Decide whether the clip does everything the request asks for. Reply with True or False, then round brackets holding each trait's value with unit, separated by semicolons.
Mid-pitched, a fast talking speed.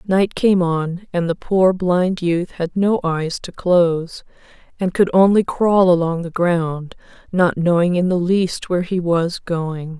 False (175 Hz; 175 wpm)